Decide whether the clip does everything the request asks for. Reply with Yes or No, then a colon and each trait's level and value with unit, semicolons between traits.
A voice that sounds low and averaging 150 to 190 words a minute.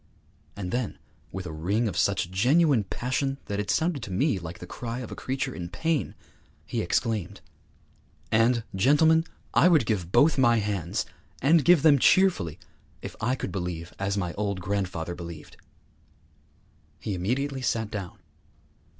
Yes: low, 110 Hz; average, 155 wpm